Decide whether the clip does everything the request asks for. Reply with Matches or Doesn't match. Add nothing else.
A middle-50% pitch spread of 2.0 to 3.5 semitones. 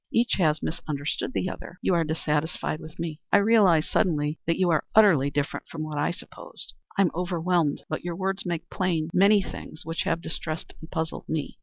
Matches